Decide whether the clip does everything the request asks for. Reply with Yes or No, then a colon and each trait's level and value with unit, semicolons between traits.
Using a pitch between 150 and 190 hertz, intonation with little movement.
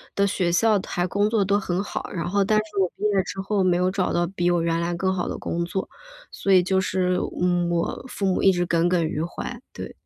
Yes: medium, 185 Hz; narrow, 2.1 semitones